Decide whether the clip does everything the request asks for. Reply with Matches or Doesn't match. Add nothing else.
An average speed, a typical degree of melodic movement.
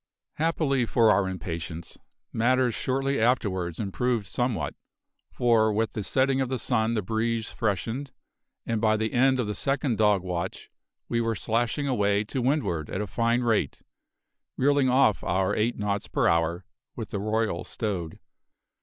Matches